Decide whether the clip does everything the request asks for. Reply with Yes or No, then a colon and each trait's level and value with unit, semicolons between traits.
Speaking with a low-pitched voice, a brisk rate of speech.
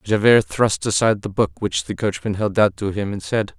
Yes: low, 105 Hz; fast, 235 wpm